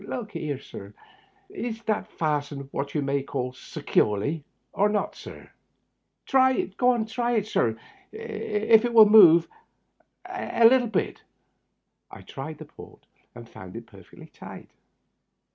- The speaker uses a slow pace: Yes, slow, 125 wpm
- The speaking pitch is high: No, medium, 180 Hz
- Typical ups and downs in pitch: No, wide, 8.5 semitones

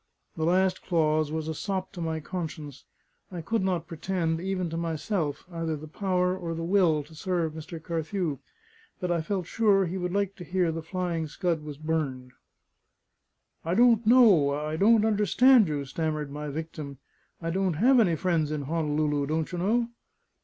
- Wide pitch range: No, average, 3.4 semitones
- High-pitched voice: No, medium, 165 Hz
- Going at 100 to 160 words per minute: No, average, 180 wpm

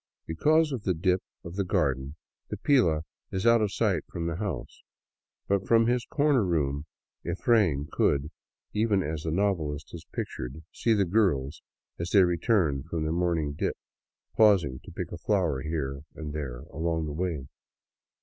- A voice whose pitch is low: Yes, very low, 85 Hz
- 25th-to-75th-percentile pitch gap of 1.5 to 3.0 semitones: No, average, 5.2 semitones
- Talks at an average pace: Yes, average, 180 wpm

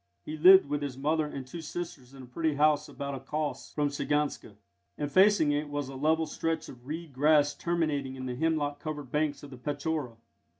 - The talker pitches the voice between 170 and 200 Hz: No, medium, 145 Hz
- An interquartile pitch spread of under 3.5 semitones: Yes, narrow, 2.4 semitones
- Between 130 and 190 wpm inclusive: No, fast, 205 wpm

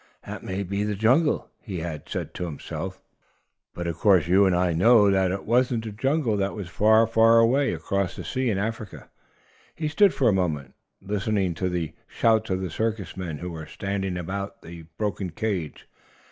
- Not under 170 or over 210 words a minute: Yes, average, 190 wpm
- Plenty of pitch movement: No, average, 4.0 semitones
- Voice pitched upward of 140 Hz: No, low, 100 Hz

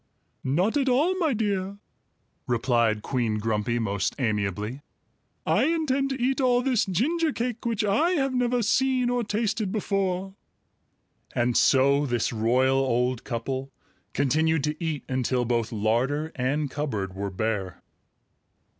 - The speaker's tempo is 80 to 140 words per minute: Yes, slow, 135 wpm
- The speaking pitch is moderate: Yes, medium, 145 Hz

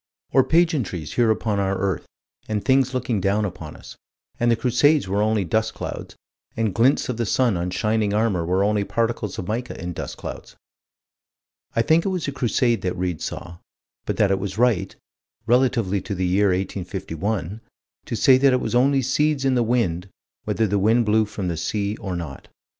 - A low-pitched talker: Yes, low, 105 Hz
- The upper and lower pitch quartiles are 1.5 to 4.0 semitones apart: No, average, 4.4 semitones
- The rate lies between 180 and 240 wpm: Yes, average, 190 wpm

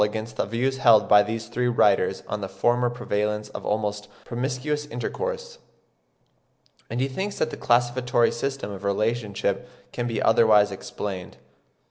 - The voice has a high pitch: No, low, 115 Hz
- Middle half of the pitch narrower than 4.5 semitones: Yes, average, 3.1 semitones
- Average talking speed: Yes, average, 150 wpm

